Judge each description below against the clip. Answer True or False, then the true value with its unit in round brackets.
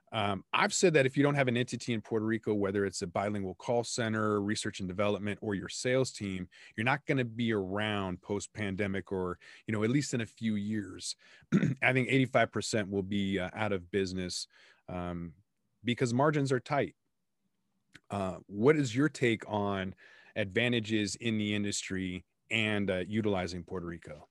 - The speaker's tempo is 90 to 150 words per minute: False (175 wpm)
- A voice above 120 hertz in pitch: False (105 Hz)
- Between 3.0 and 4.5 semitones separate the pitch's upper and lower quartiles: True (3.7 semitones)